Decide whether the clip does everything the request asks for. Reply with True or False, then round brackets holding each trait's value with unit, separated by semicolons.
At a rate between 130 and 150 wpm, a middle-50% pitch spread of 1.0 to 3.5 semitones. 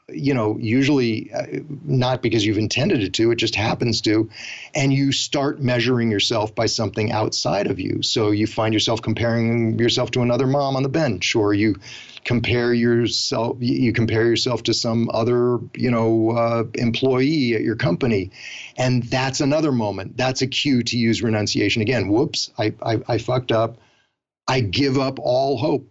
False (170 wpm; 2.4 semitones)